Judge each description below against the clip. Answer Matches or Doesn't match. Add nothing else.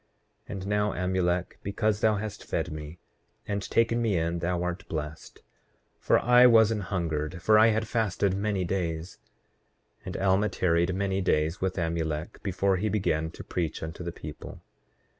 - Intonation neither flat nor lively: Matches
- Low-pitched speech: Matches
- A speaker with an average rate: Matches